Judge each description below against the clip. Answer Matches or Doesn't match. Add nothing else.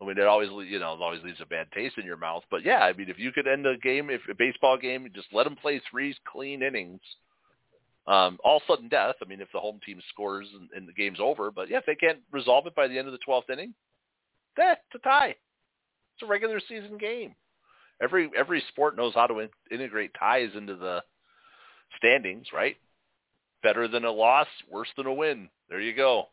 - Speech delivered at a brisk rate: Matches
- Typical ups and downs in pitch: Doesn't match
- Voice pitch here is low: Matches